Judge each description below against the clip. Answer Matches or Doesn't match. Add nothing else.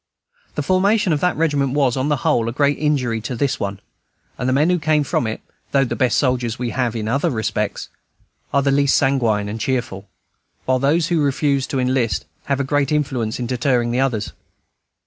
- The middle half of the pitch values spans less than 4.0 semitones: Matches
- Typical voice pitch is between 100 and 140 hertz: Matches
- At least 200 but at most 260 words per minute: Matches